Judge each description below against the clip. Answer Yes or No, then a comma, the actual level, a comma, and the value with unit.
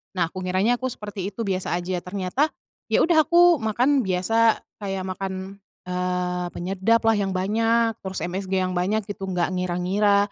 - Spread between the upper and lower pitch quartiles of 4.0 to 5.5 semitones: No, average, 3.5 semitones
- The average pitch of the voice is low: No, high, 195 Hz